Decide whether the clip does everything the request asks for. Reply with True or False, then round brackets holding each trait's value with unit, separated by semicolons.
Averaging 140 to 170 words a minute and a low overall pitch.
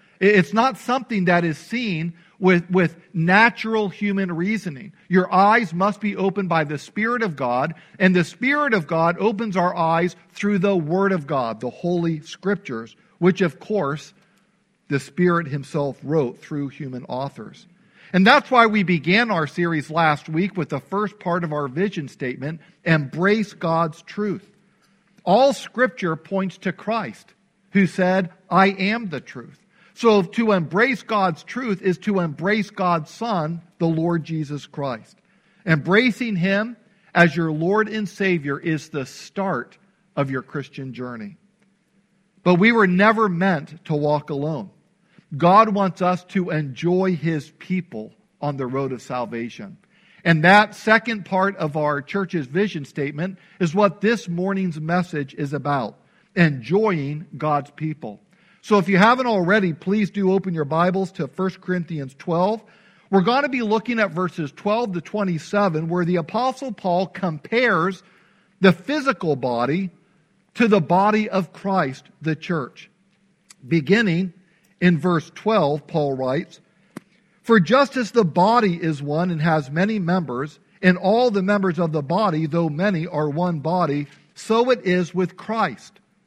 False (150 wpm; 185 Hz)